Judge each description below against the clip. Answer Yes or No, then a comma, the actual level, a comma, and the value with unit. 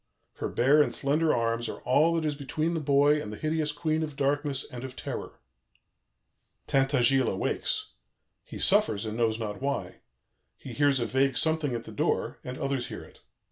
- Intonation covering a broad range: No, average, 3.4 semitones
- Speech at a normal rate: Yes, average, 180 wpm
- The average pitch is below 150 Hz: Yes, medium, 140 Hz